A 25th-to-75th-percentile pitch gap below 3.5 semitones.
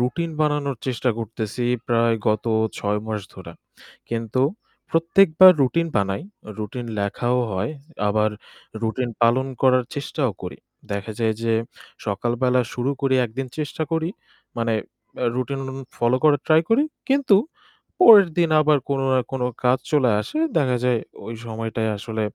No: average, 4.3 semitones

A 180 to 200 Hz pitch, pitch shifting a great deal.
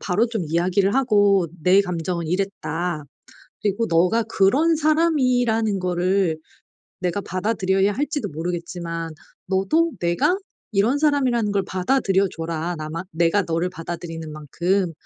No: high, 190 Hz; average, 4.7 semitones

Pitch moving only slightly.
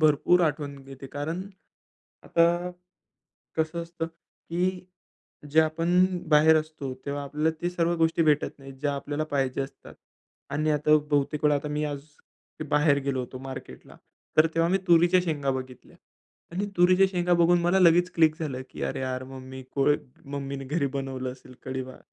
No: average, 3.5 semitones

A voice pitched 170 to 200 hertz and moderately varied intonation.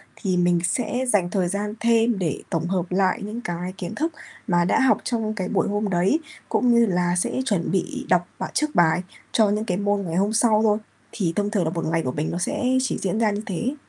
Yes: high, 195 Hz; average, 3.8 semitones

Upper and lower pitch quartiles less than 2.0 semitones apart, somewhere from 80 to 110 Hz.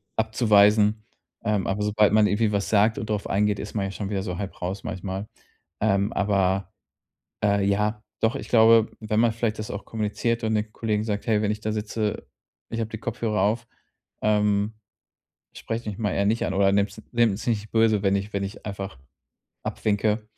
Yes: narrow, 1.6 semitones; low, 105 Hz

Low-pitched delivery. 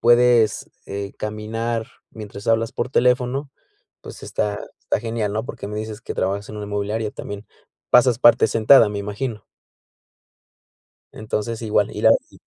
Yes: low, 110 Hz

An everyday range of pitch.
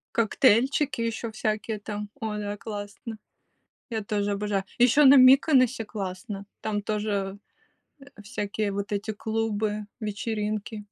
No: narrow, 1.9 semitones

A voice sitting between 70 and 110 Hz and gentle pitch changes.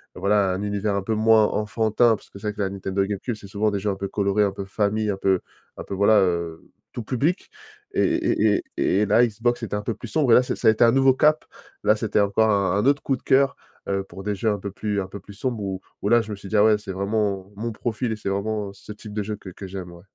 Yes: low, 105 Hz; narrow, 2.0 semitones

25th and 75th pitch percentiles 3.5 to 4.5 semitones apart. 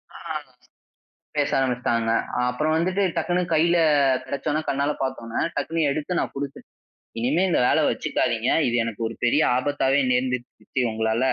Yes: average, 4.0 semitones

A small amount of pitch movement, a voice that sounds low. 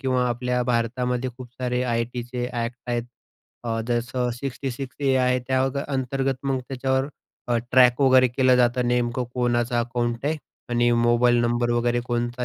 Yes: narrow, 1.2 semitones; low, 125 Hz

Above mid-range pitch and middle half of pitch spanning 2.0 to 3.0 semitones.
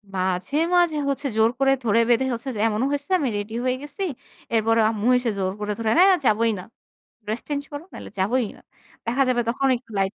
No: high, 230 Hz; average, 4.3 semitones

